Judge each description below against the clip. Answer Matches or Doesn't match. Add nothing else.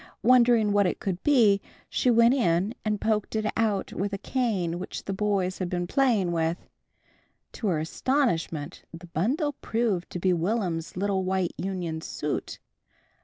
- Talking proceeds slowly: Doesn't match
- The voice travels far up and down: Doesn't match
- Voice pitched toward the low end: Doesn't match